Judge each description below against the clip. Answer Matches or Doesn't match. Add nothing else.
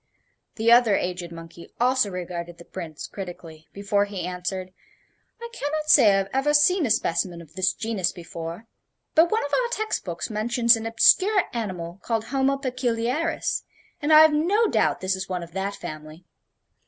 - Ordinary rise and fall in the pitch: Doesn't match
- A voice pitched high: Matches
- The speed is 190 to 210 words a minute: Doesn't match